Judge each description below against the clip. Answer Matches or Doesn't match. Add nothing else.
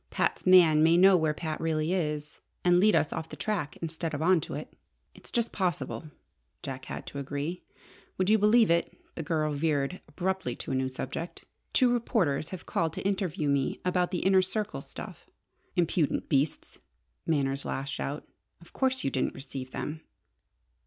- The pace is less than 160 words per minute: Doesn't match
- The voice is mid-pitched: Matches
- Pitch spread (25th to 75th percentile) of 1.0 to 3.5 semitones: Doesn't match